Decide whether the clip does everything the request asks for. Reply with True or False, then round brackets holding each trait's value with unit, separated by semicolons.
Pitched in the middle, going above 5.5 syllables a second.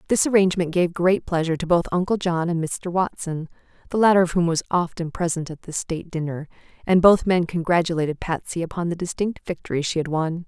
True (170 Hz; 5.9 syllables/s)